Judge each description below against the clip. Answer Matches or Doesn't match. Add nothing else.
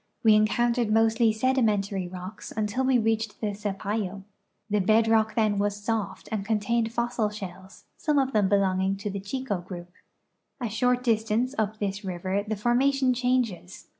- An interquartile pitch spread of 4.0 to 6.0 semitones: Doesn't match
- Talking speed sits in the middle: Matches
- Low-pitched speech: Doesn't match